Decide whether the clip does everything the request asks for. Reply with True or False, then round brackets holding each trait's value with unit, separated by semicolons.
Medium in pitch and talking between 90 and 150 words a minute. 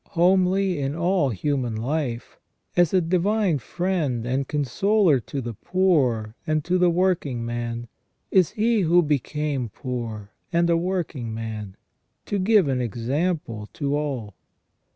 True (150 Hz; 140 wpm)